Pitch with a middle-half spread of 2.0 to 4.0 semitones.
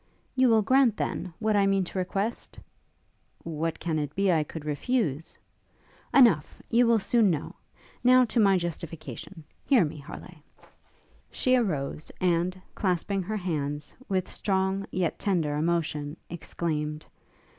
No: average, 5.1 semitones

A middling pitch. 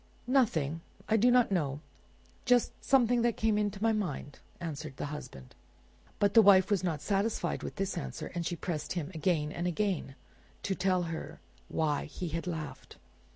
Yes: medium, 180 Hz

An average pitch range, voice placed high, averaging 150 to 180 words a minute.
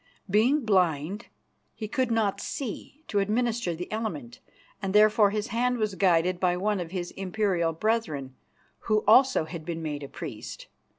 Yes: average, 4.3 semitones; high, 200 Hz; average, 160 wpm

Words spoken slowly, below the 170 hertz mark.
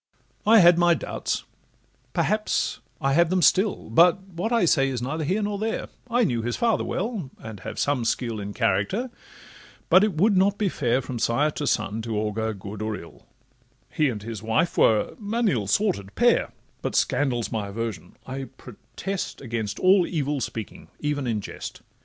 No: average, 175 wpm; low, 135 Hz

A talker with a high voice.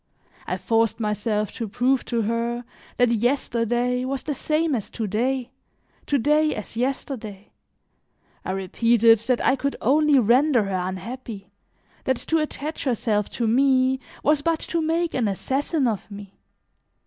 Yes: high, 245 Hz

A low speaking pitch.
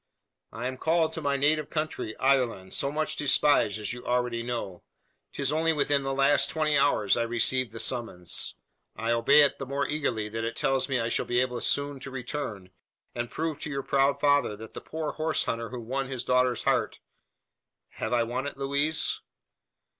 Yes: low, 130 Hz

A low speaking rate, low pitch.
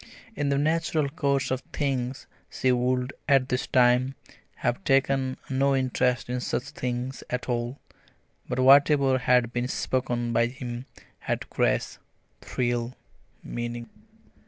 Yes: slow, 130 wpm; low, 130 Hz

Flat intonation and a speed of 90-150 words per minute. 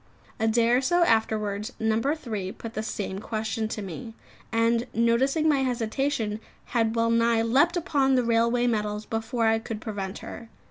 No: narrow, 2.1 semitones; average, 170 wpm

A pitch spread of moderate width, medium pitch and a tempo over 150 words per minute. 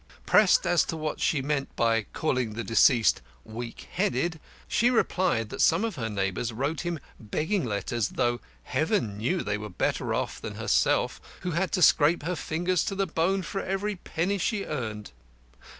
No: wide, 8.0 semitones; medium, 155 Hz; average, 175 wpm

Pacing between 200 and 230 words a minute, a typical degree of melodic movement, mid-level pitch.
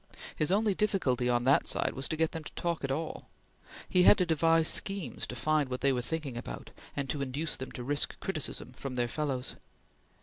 Yes: fast, 205 wpm; average, 4.2 semitones; medium, 145 Hz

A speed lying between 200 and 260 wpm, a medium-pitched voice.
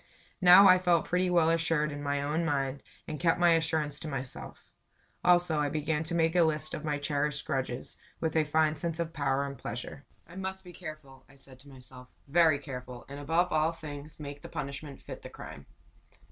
Yes: fast, 205 wpm; medium, 150 Hz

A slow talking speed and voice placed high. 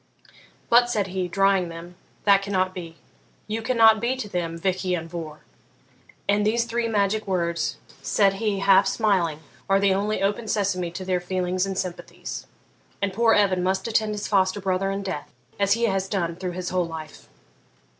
No: average, 175 wpm; high, 195 Hz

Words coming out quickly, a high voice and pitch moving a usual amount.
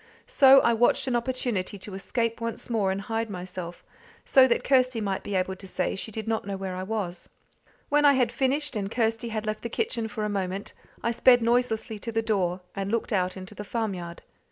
Yes: fast, 215 wpm; high, 220 Hz; average, 3.5 semitones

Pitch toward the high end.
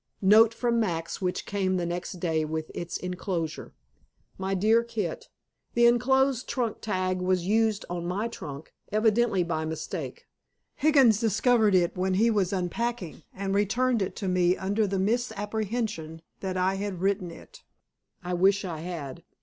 Yes: high, 195 Hz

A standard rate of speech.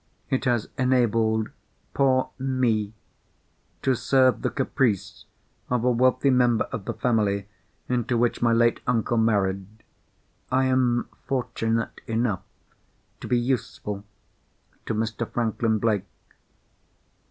No: slow, 115 wpm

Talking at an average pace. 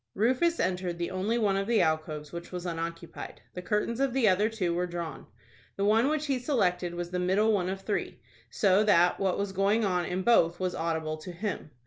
No: fast, 210 wpm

